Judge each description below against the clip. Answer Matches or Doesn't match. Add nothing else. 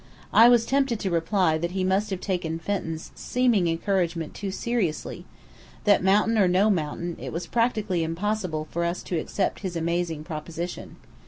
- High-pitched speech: Doesn't match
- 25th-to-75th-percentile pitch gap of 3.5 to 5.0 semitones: Matches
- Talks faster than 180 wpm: Doesn't match